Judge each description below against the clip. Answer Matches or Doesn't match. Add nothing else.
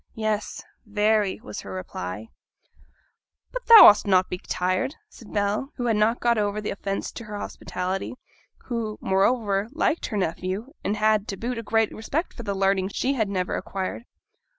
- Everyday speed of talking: Matches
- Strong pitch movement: Doesn't match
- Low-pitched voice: Doesn't match